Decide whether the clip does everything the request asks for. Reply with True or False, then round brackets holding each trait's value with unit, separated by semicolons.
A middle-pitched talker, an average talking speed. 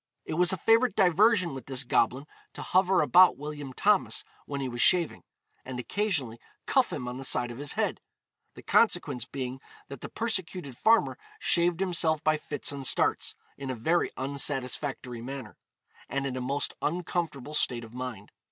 True (145 Hz; 170 wpm)